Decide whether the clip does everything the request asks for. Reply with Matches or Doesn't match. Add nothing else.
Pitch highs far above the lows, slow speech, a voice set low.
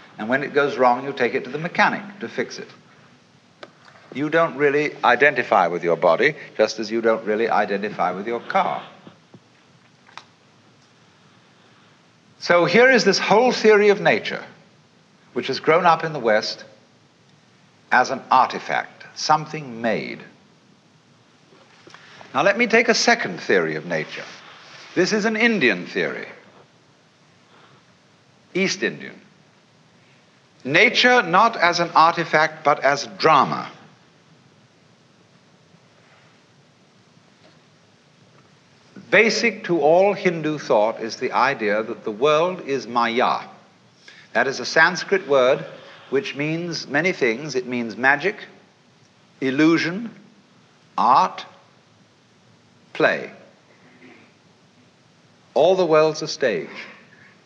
Doesn't match